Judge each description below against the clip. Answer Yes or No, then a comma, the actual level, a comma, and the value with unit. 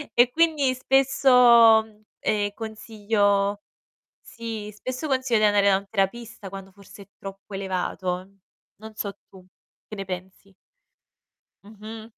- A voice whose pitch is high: Yes, high, 210 Hz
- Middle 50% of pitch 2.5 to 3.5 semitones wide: Yes, average, 2.8 semitones